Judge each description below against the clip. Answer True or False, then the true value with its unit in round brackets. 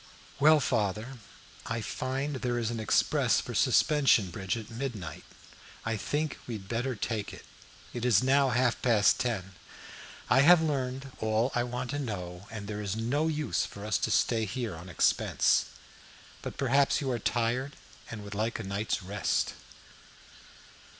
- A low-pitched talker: True (115 Hz)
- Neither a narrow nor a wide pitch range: True (4.1 semitones)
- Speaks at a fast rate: False (165 wpm)